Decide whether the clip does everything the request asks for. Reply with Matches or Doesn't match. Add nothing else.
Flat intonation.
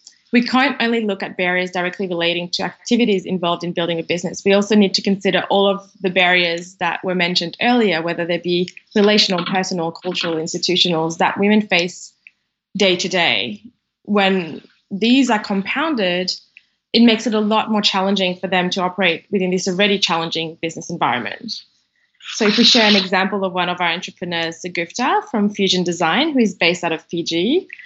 Doesn't match